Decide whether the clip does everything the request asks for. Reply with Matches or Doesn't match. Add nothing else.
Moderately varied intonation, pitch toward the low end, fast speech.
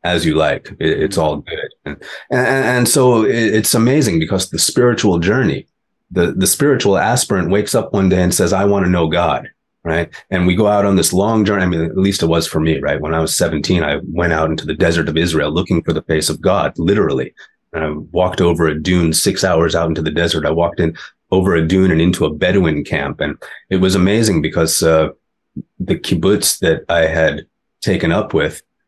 Matches